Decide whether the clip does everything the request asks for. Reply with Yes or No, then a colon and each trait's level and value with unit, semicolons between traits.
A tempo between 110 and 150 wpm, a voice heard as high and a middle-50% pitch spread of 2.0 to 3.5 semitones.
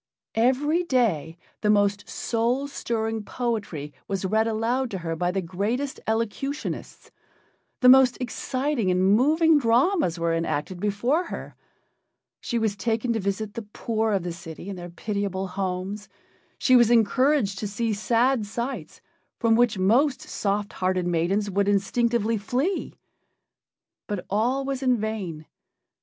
No: average, 140 wpm; high, 220 Hz; average, 4.2 semitones